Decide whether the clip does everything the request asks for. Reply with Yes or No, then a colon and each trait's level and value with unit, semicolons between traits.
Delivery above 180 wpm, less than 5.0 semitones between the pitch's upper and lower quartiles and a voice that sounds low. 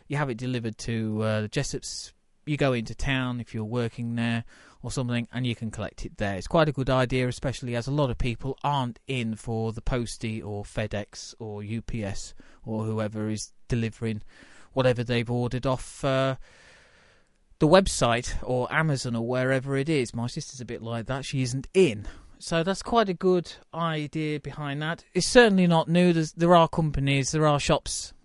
Yes: average, 190 wpm; average, 4.5 semitones; low, 125 Hz